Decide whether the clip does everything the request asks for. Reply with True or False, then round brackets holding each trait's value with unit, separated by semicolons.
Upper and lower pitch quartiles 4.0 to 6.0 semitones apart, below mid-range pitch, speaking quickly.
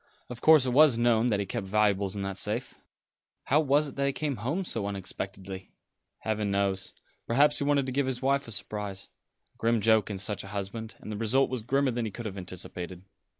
True (5.0 semitones; 110 Hz; 220 wpm)